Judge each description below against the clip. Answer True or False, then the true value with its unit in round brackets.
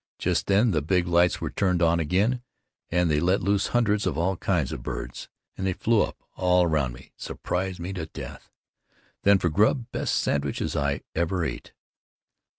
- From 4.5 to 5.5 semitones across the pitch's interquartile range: False (3.3 semitones)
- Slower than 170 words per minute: False (180 wpm)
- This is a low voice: True (90 Hz)